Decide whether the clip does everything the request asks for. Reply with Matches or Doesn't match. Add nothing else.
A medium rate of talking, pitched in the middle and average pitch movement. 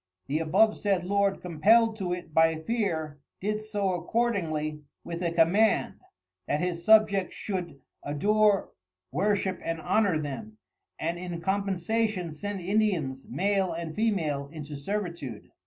Doesn't match